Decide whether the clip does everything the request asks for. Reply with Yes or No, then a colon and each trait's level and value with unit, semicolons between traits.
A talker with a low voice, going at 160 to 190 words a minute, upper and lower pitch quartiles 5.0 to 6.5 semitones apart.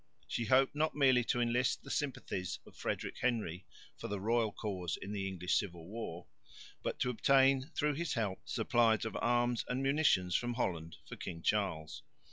Yes: low, 115 Hz; average, 175 wpm; average, 5.3 semitones